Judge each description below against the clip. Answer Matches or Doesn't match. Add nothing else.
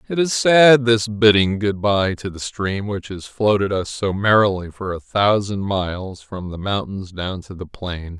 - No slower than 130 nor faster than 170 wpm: Doesn't match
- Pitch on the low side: Matches